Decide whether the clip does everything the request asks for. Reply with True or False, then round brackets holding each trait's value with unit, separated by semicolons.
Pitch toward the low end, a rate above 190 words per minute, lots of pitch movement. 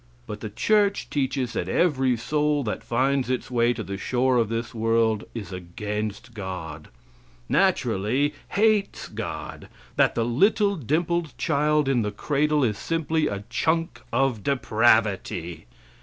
False (125 Hz; 140 wpm; 5.8 semitones)